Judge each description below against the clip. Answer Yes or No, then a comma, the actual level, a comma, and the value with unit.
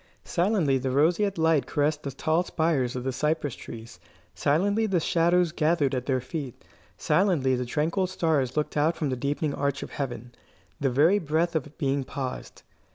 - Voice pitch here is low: No, medium, 150 Hz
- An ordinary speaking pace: Yes, average, 170 wpm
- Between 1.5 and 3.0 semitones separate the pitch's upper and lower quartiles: No, average, 3.9 semitones